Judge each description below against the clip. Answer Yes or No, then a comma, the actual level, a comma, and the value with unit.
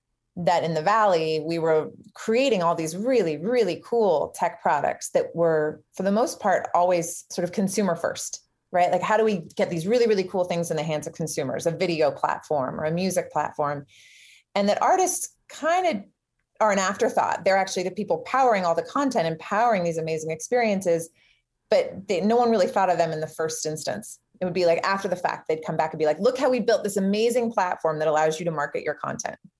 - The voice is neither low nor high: Yes, medium, 180 Hz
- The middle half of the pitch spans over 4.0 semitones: Yes, average, 5.3 semitones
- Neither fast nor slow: No, fast, 220 wpm